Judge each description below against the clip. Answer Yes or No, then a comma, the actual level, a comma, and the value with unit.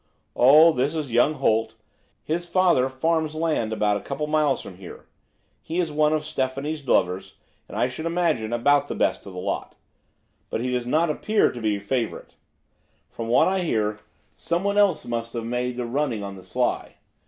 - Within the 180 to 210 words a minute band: Yes, average, 190 wpm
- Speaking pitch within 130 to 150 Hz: Yes, low, 135 Hz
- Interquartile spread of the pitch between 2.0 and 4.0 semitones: No, wide, 5.4 semitones